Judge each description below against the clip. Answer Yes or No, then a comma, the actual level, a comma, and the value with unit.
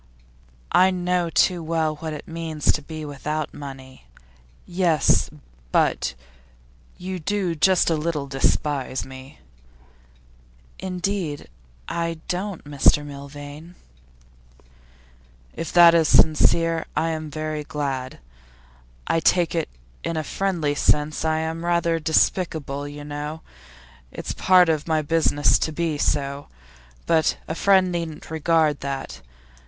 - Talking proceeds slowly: Yes, slow, 120 wpm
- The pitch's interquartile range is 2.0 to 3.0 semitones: Yes, narrow, 2.6 semitones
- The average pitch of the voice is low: No, medium, 160 Hz